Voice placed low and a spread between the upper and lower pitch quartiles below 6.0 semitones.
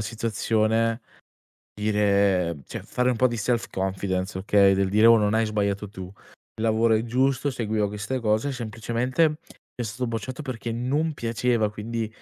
Yes: low, 110 Hz; narrow, 2.4 semitones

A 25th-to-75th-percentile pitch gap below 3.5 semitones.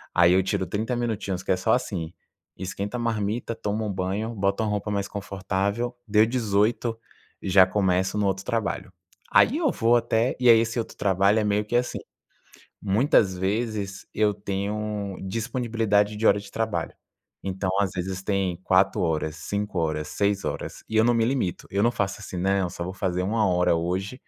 Yes: average, 2.9 semitones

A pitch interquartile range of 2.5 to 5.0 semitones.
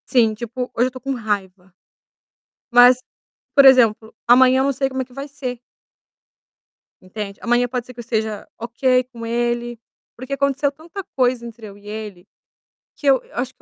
Yes: average, 2.9 semitones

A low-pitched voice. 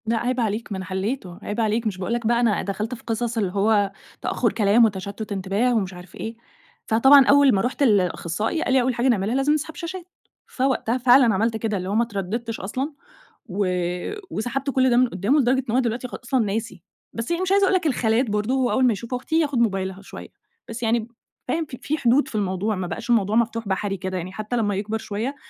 No: high, 230 Hz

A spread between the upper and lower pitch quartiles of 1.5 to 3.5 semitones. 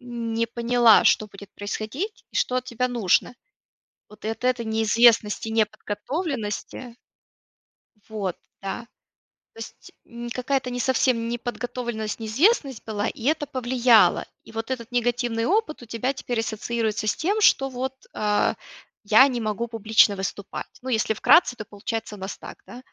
Yes: narrow, 2.5 semitones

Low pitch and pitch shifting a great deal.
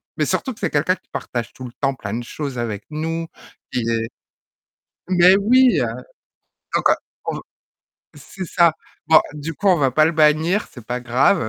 No: medium, 150 Hz; wide, 6.3 semitones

